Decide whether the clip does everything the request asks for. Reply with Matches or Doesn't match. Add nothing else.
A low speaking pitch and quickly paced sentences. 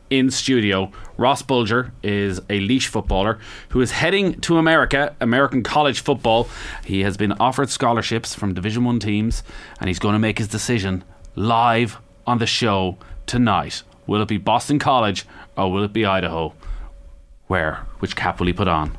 Doesn't match